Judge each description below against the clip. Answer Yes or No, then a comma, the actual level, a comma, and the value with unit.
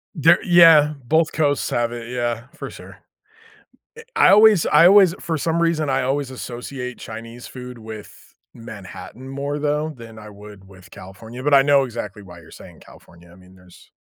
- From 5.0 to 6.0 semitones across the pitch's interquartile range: Yes, average, 5.3 semitones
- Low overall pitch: Yes, low, 125 Hz